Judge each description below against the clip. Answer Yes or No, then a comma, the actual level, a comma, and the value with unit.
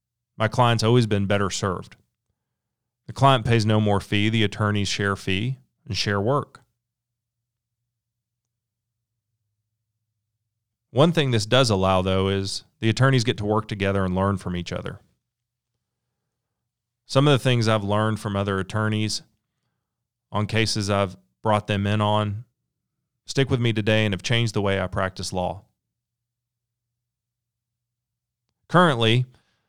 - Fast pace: No, slow, 135 wpm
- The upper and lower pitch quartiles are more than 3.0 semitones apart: No, narrow, 2.5 semitones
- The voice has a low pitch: Yes, low, 115 Hz